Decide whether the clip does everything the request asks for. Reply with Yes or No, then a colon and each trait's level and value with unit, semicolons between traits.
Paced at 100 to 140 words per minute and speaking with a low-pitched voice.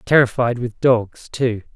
Yes: slow, 135 wpm; low, 120 Hz